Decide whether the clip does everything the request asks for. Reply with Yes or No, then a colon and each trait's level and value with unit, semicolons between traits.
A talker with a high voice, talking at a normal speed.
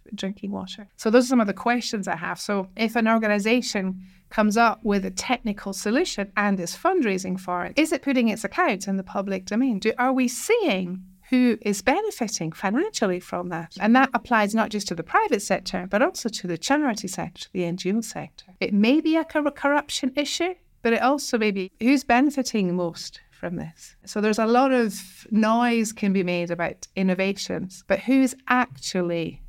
Yes: high, 215 Hz; average, 190 wpm